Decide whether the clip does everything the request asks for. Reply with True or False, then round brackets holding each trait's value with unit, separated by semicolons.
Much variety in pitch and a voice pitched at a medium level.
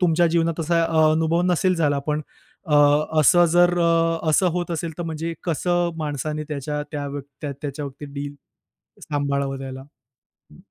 False (2.7 semitones; 155 Hz)